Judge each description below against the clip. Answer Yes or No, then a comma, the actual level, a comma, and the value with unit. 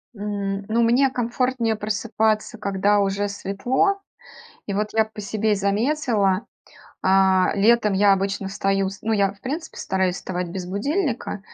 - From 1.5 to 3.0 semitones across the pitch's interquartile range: Yes, average, 2.7 semitones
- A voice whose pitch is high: Yes, high, 205 Hz